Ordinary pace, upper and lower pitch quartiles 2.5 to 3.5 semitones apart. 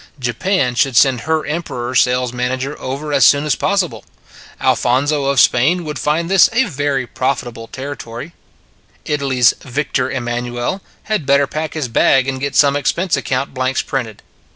Yes: average, 160 wpm; average, 3.2 semitones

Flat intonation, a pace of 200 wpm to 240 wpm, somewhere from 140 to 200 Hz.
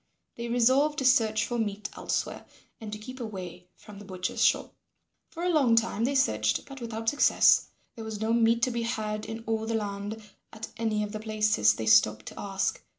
No: narrow, 2.3 semitones; fast, 205 wpm; high, 220 Hz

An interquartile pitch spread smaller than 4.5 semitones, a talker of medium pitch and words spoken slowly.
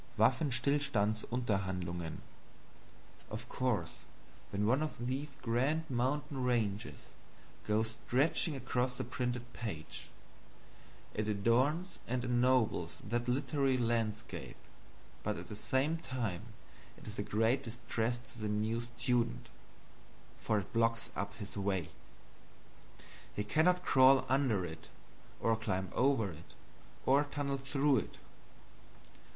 No: average, 3.8 semitones; low, 120 Hz; slow, 115 wpm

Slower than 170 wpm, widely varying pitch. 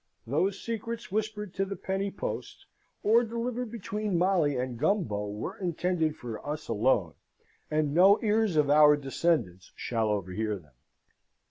Yes: average, 140 wpm; wide, 9.0 semitones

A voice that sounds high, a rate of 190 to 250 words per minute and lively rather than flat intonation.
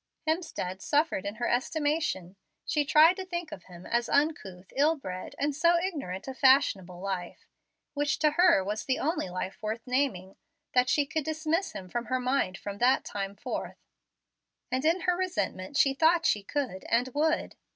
No: very high, 265 Hz; average, 175 wpm; wide, 8.0 semitones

